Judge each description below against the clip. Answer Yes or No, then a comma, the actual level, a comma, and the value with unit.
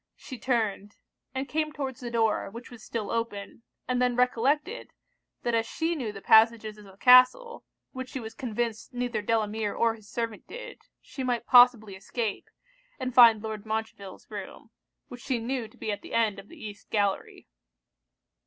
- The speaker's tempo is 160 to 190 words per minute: Yes, average, 175 wpm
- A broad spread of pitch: No, average, 2.8 semitones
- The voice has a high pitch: Yes, high, 230 Hz